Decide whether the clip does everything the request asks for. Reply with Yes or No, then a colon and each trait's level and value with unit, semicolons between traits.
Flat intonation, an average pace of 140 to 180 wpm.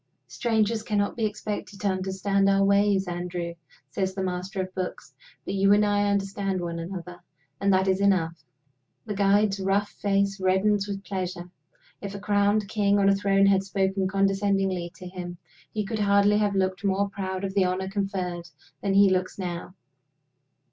Yes: narrow, 1.3 semitones; average, 170 wpm